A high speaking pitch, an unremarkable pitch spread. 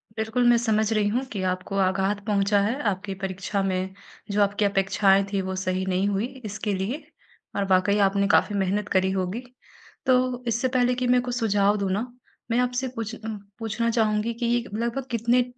Yes: high, 210 Hz; average, 3.3 semitones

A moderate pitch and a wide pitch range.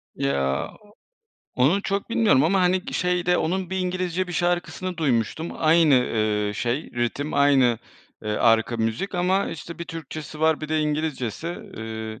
Yes: medium, 155 Hz; wide, 7.0 semitones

